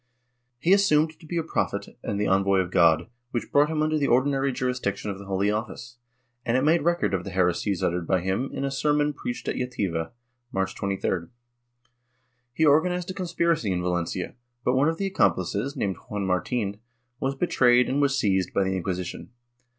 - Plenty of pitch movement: Yes, wide, 7.6 semitones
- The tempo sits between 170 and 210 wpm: Yes, average, 190 wpm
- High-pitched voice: No, low, 120 Hz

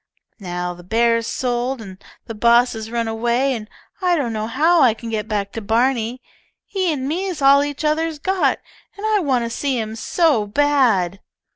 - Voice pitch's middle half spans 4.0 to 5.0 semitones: Yes, average, 4.7 semitones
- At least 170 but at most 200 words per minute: Yes, average, 185 wpm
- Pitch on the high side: Yes, high, 240 Hz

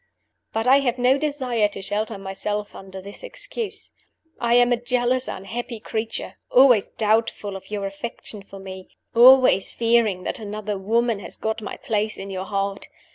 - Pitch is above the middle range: Yes, high, 220 Hz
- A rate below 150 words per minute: No, average, 165 wpm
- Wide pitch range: No, average, 3.5 semitones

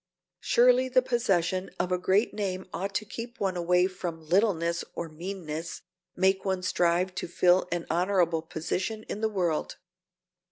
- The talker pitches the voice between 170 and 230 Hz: Yes, medium, 185 Hz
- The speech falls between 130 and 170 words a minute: Yes, average, 155 wpm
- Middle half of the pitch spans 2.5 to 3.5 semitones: Yes, average, 2.8 semitones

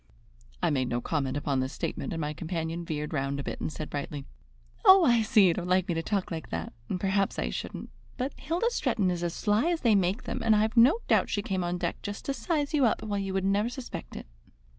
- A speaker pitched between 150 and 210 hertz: Yes, high, 190 Hz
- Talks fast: Yes, fast, 250 wpm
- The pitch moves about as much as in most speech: No, wide, 6.1 semitones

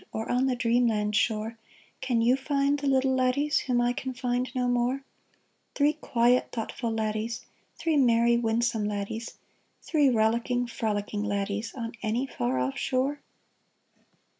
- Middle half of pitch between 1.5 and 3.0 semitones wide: Yes, average, 2.7 semitones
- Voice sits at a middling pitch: No, high, 240 Hz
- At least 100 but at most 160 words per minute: Yes, average, 140 wpm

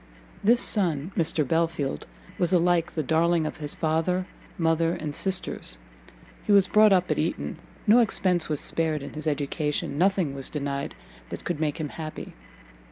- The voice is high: No, medium, 165 Hz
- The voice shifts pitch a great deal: No, average, 3.3 semitones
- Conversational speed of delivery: Yes, average, 165 wpm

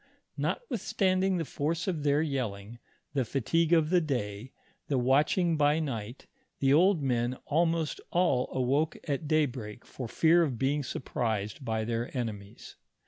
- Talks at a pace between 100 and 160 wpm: Yes, average, 140 wpm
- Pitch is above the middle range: No, medium, 140 Hz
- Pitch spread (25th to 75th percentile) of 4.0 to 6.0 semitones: Yes, average, 5.1 semitones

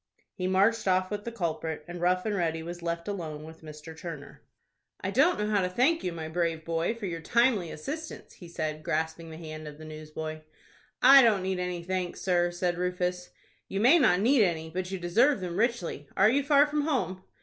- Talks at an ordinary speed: No, fast, 210 wpm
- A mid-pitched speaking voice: Yes, medium, 180 Hz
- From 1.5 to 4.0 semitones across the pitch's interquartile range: No, average, 4.4 semitones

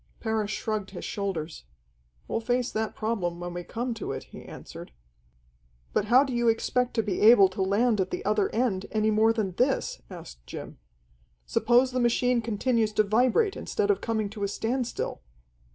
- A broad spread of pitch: No, average, 3.4 semitones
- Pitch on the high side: Yes, high, 220 Hz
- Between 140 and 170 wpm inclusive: No, average, 180 wpm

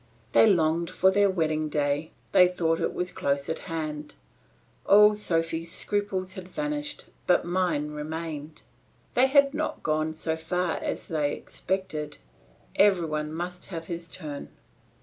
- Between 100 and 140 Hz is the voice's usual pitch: No, medium, 165 Hz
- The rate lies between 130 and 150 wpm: Yes, average, 145 wpm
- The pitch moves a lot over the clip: No, average, 3.4 semitones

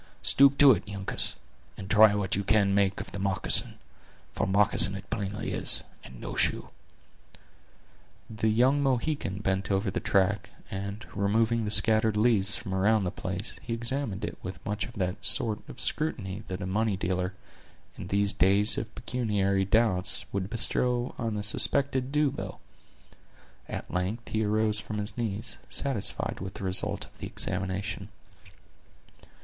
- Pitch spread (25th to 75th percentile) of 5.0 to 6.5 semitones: No, average, 2.7 semitones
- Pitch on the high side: No, low, 105 Hz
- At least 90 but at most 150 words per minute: No, average, 160 wpm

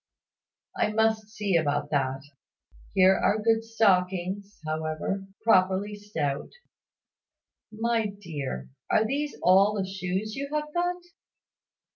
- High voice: Yes, high, 200 Hz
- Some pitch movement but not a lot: Yes, average, 4.1 semitones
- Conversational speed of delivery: No, slow, 110 wpm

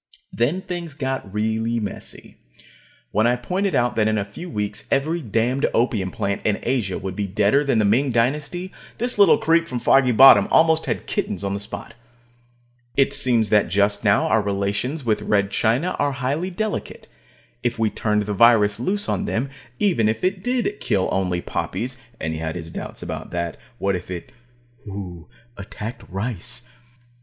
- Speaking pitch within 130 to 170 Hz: No, low, 115 Hz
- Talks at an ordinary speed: Yes, average, 175 wpm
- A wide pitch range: Yes, wide, 5.9 semitones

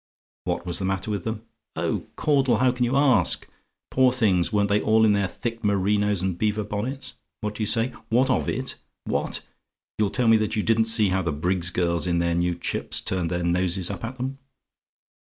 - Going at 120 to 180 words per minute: No, fast, 205 wpm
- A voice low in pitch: Yes, low, 105 Hz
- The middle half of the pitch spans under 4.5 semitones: Yes, average, 4.0 semitones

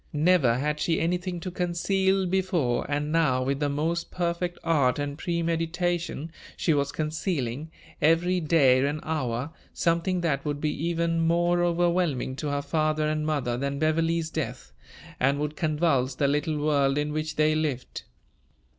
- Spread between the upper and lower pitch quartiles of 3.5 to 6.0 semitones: No, average, 3.0 semitones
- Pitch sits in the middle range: Yes, medium, 155 Hz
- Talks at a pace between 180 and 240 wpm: No, average, 155 wpm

